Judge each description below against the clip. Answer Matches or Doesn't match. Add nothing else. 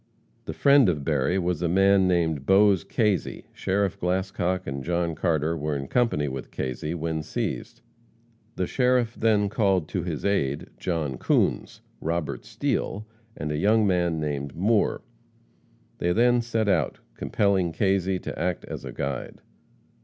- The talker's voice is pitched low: Matches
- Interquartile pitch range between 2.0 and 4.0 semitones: Doesn't match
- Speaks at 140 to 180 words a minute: Matches